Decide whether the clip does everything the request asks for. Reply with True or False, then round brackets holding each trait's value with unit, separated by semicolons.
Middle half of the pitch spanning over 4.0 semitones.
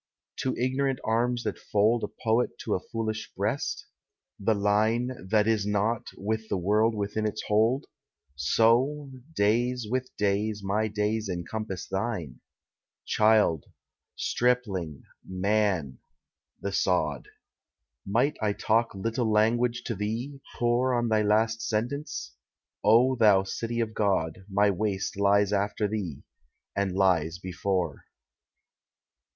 False (2.9 semitones)